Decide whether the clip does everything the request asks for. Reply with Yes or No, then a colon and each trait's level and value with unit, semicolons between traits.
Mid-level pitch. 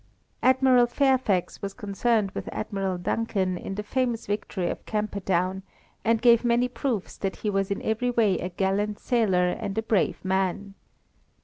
No: high, 205 Hz